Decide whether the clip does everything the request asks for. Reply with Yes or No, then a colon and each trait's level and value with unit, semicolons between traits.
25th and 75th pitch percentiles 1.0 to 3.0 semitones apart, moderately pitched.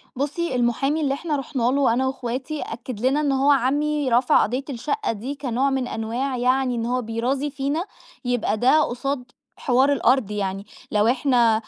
No: average, 2.7 semitones; very high, 260 Hz